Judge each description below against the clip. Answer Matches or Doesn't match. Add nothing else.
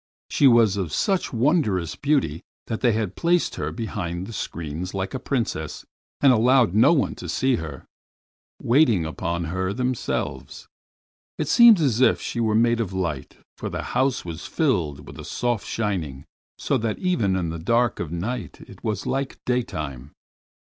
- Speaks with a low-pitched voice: Matches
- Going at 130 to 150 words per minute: Doesn't match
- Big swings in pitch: Matches